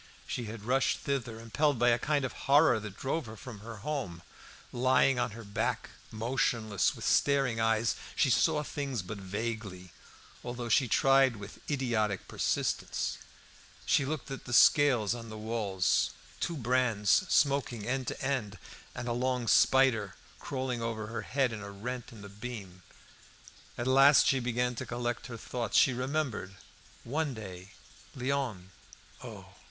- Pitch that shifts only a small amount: No, average, 3.6 semitones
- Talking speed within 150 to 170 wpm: Yes, average, 160 wpm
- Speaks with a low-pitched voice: Yes, low, 120 Hz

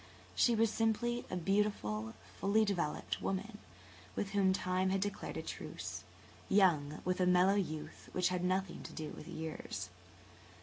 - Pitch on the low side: No, medium, 185 Hz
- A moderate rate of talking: Yes, average, 155 wpm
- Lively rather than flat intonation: No, average, 4.1 semitones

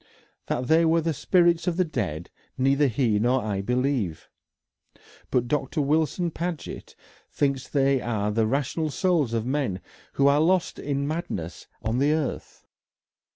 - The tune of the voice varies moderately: Yes, average, 4.9 semitones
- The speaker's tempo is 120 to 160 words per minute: Yes, average, 150 wpm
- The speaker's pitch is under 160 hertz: Yes, medium, 140 Hz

